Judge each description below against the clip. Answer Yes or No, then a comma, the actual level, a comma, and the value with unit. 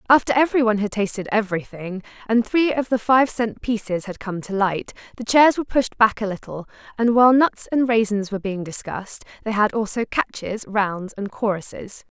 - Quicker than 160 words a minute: Yes, average, 190 wpm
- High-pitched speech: Yes, high, 220 Hz